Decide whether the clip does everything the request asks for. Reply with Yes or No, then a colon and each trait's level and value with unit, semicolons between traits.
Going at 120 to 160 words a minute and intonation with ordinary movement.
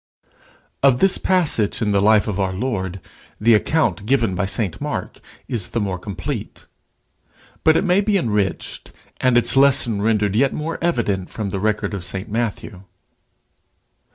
Yes: average, 155 wpm; average, 4.7 semitones